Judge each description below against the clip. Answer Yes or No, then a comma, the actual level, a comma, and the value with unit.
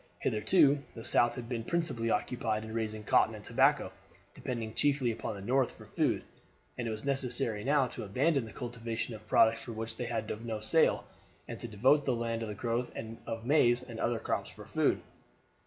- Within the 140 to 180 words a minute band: No, average, 195 wpm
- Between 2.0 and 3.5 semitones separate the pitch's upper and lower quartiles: Yes, narrow, 2.5 semitones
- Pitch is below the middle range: Yes, low, 115 Hz